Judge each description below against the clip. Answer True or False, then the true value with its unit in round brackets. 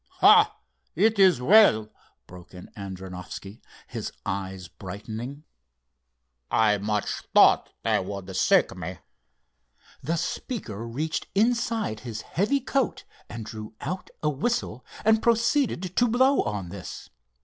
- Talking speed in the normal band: False (120 wpm)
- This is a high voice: False (115 Hz)